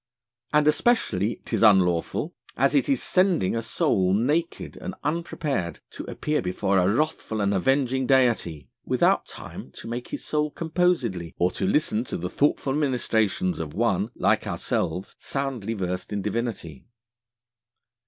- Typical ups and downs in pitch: No, wide, 8.1 semitones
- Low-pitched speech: Yes, low, 115 Hz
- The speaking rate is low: No, average, 145 wpm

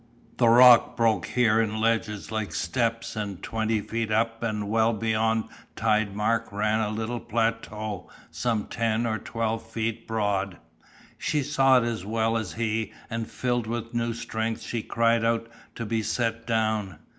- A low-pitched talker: Yes, low, 115 Hz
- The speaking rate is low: No, average, 160 wpm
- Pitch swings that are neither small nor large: No, narrow, 1.1 semitones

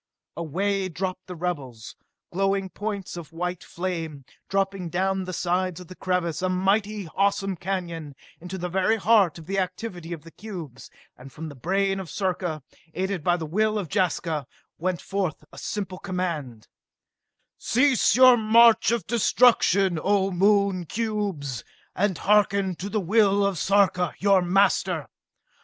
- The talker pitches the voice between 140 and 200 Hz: Yes, medium, 185 Hz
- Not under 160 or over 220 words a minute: No, average, 150 wpm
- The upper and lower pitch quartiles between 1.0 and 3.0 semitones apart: Yes, average, 2.7 semitones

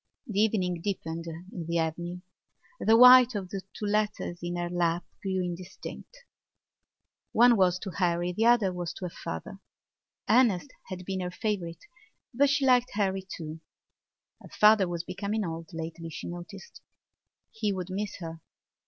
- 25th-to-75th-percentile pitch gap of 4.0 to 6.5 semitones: No, average, 3.5 semitones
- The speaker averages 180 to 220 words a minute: No, average, 155 wpm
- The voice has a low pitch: No, medium, 185 Hz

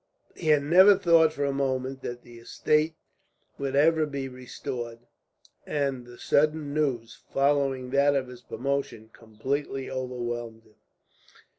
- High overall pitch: No, low, 135 Hz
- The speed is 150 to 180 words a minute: No, slow, 135 wpm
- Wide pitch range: No, average, 2.9 semitones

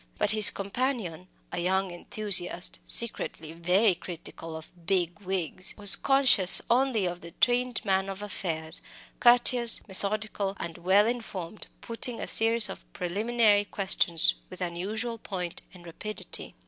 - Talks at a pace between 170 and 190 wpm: No, slow, 135 wpm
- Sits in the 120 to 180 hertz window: No, high, 195 Hz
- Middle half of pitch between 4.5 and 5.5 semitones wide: No, average, 4.1 semitones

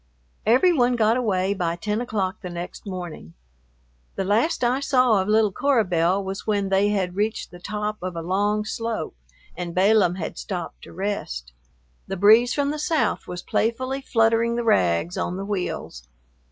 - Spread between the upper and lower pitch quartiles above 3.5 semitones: Yes, average, 4.0 semitones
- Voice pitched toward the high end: Yes, high, 205 Hz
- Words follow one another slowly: No, average, 175 wpm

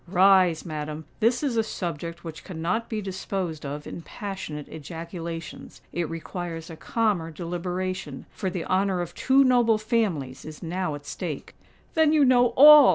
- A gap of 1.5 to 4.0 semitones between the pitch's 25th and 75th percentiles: No, average, 4.8 semitones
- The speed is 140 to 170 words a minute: Yes, average, 150 wpm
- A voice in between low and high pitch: Yes, medium, 180 Hz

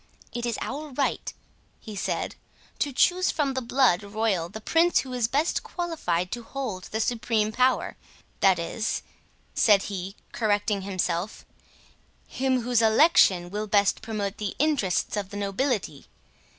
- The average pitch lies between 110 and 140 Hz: No, high, 220 Hz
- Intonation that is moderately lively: Yes, average, 4.8 semitones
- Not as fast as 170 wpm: Yes, average, 140 wpm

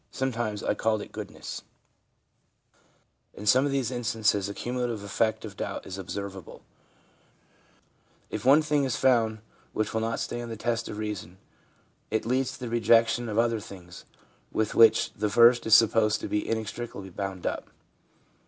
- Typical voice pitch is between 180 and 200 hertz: No, low, 110 Hz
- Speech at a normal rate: Yes, average, 160 wpm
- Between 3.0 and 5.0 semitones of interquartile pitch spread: No, narrow, 2.4 semitones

